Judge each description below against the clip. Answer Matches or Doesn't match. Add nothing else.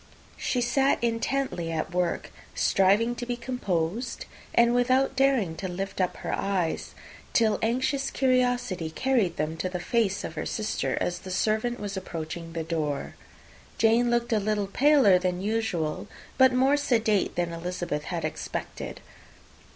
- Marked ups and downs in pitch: Matches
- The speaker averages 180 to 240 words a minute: Doesn't match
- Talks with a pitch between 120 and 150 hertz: Doesn't match